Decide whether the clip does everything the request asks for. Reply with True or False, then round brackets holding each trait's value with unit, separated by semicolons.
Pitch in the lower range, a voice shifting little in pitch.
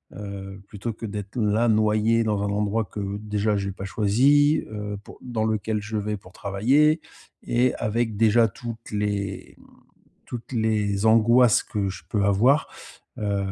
True (105 Hz; 2.1 semitones)